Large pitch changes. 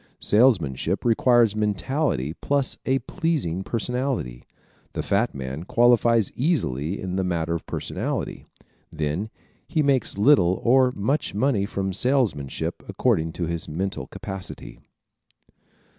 Yes: wide, 7.1 semitones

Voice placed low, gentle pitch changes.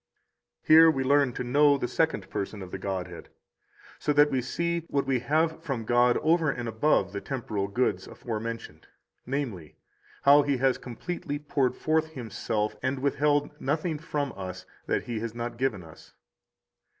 No: low, 130 Hz; average, 4.6 semitones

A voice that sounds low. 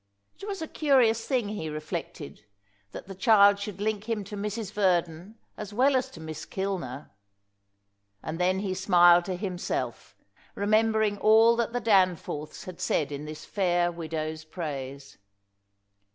No: high, 190 Hz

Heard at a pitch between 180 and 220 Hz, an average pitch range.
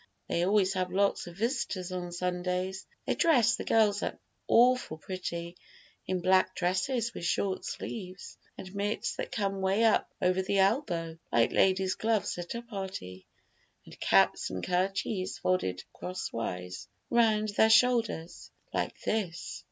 Yes: high, 190 Hz; average, 3.2 semitones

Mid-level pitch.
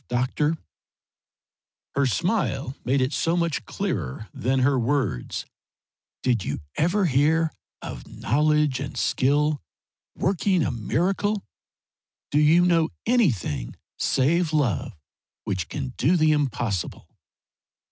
Yes: medium, 145 Hz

